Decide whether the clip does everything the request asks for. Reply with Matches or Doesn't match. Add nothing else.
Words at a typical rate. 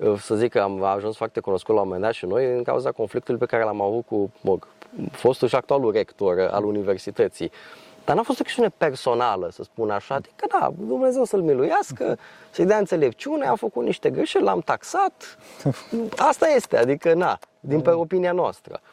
Doesn't match